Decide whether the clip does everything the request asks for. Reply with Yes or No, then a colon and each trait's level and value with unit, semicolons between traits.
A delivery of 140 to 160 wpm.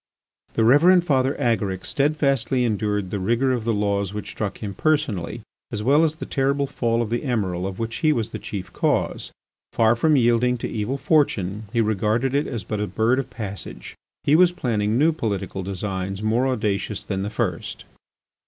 No: average, 185 wpm